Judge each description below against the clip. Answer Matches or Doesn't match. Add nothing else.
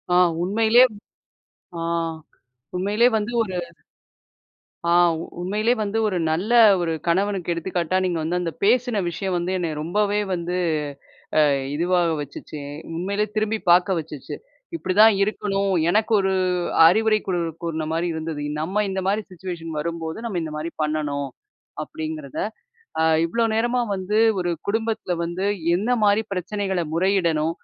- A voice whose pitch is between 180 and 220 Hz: Matches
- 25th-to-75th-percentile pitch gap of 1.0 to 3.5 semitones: Doesn't match